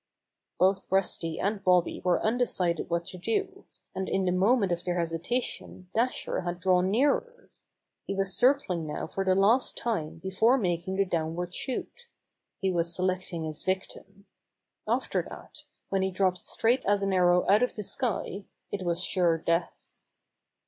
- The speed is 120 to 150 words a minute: No, average, 165 wpm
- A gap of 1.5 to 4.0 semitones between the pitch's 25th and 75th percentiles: Yes, average, 2.9 semitones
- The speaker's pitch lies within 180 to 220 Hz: Yes, high, 190 Hz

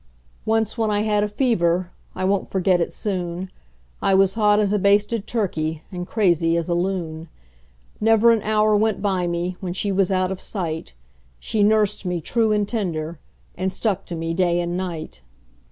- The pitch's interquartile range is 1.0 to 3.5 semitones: Yes, average, 3.2 semitones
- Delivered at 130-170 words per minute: No, average, 185 wpm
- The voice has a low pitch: No, high, 190 Hz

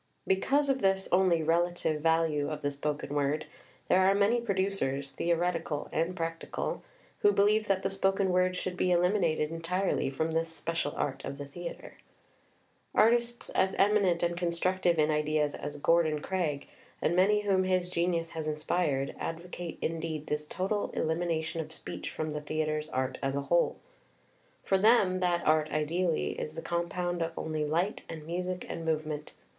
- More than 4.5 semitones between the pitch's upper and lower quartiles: No, average, 3.2 semitones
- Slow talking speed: No, average, 165 wpm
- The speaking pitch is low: No, medium, 170 Hz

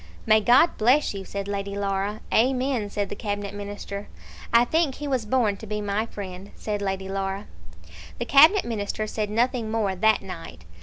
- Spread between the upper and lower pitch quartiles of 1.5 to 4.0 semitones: Yes, average, 2.8 semitones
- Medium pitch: No, high, 210 Hz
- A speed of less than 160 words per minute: No, average, 175 wpm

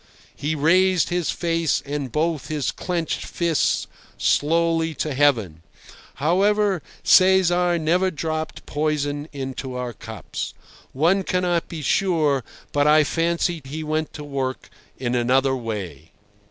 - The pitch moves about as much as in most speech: Yes, average, 3.8 semitones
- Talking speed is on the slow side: Yes, slow, 125 wpm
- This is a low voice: No, medium, 155 Hz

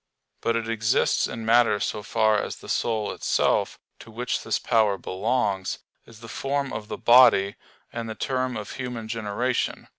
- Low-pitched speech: Yes, low, 115 Hz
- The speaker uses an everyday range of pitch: No, narrow, 2.2 semitones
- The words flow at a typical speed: Yes, average, 170 wpm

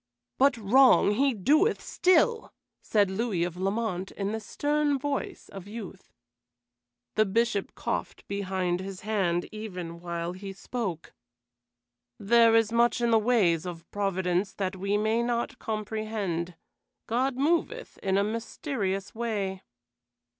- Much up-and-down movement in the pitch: No, average, 3.8 semitones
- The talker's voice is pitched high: Yes, high, 210 Hz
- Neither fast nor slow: No, slow, 130 wpm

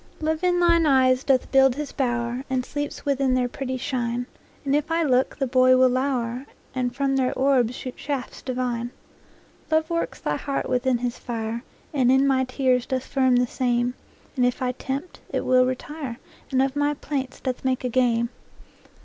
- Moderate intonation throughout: No, narrow, 1.8 semitones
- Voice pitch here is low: No, very high, 260 Hz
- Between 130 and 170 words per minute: No, average, 185 wpm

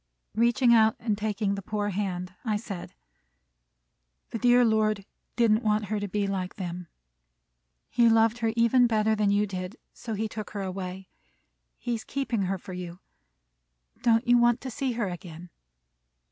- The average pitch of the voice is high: Yes, high, 215 Hz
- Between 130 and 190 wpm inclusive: Yes, average, 165 wpm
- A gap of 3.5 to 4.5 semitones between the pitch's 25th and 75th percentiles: No, average, 3.0 semitones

